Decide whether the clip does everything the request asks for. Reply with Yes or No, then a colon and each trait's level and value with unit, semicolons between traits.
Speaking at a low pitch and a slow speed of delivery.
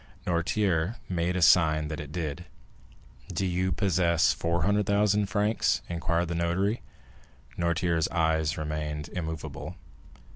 Yes: very low, 85 Hz; slow, 110 wpm